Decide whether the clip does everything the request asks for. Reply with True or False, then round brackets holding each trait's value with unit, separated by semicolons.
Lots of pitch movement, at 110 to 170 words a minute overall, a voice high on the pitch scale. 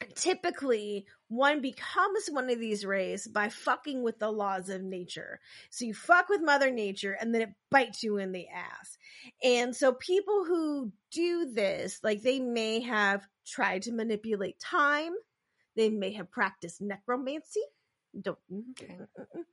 True (6.0 semitones; 150 wpm; 230 Hz)